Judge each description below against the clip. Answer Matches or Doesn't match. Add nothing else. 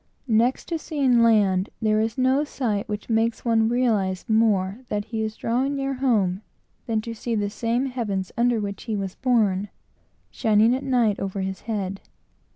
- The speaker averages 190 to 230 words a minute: Doesn't match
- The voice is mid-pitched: Doesn't match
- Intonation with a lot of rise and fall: Doesn't match